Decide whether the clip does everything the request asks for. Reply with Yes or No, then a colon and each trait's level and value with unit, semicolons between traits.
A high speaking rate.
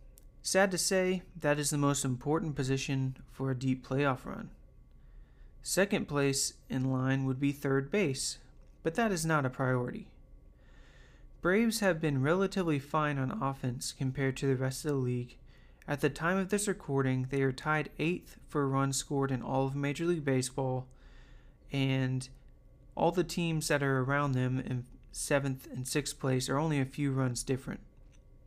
No: average, 170 wpm